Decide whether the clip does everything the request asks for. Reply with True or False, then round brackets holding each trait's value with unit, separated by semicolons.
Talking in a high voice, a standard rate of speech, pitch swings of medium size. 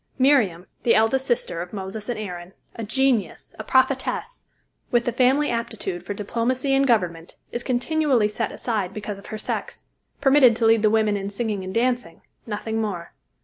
True (225 Hz; 175 wpm; 4.0 semitones)